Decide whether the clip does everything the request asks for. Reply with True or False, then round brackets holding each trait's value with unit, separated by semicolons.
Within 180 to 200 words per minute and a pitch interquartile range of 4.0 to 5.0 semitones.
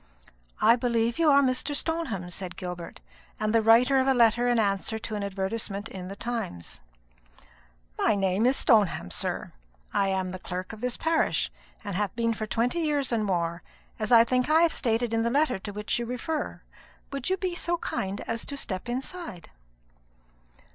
True (190 wpm; 4.5 semitones)